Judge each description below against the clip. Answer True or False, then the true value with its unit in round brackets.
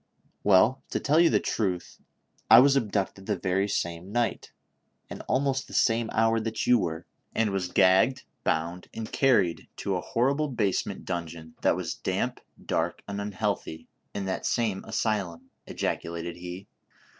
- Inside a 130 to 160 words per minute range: True (155 wpm)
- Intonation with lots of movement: False (4.2 semitones)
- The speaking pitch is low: True (100 Hz)